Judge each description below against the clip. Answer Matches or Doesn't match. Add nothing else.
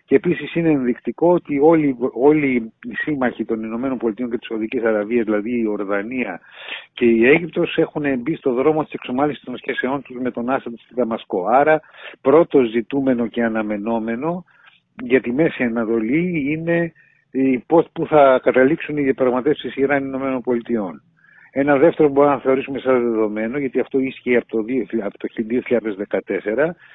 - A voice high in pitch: Doesn't match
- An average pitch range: Matches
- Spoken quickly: Doesn't match